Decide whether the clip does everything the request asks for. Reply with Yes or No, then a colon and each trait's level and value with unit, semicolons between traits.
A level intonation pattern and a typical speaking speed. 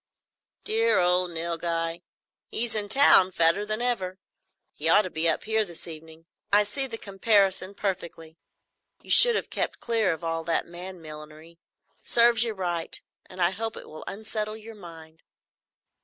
No: average, 4.6 semitones; average, 160 wpm